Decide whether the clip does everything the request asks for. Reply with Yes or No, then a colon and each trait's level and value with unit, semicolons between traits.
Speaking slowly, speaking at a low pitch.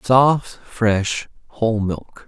Yes: slow, 105 wpm; low, 115 Hz